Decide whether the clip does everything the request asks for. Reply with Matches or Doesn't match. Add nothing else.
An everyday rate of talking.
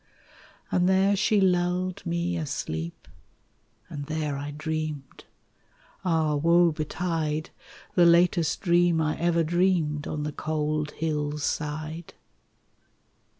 Doesn't match